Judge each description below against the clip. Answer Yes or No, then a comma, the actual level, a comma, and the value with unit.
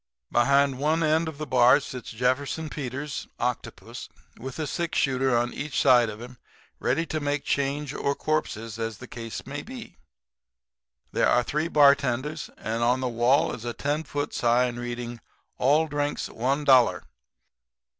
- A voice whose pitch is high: No, low, 135 Hz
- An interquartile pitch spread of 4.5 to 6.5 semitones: No, average, 3.5 semitones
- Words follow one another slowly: No, average, 155 wpm